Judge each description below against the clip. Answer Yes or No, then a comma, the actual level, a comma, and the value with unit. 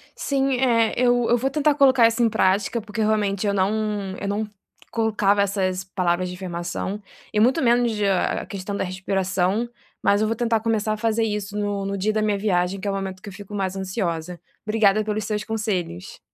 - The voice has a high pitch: Yes, high, 205 Hz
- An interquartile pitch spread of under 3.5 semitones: Yes, average, 2.7 semitones